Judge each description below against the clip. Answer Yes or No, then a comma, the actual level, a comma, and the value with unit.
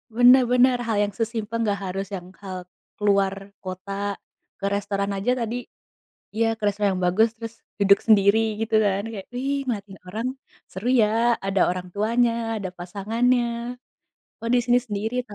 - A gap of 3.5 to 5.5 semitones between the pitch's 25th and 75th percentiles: No, average, 2.9 semitones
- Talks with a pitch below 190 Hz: No, high, 210 Hz